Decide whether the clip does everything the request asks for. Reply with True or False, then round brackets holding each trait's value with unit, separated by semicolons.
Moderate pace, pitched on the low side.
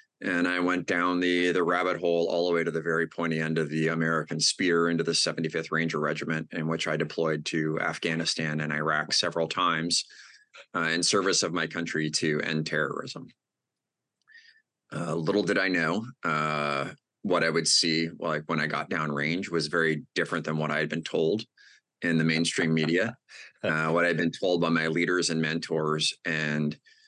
True (190 wpm; 80 Hz)